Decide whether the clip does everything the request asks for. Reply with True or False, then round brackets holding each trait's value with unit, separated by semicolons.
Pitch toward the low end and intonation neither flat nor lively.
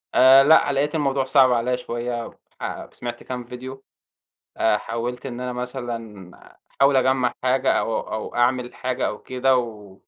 False (125 Hz; 1.8 semitones)